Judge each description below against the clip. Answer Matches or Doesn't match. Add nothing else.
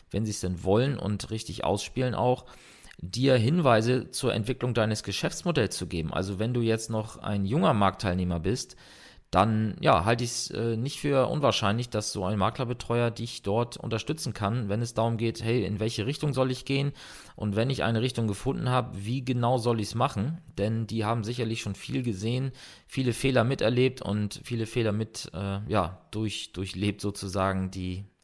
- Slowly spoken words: Doesn't match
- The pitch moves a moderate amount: Matches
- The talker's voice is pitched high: Doesn't match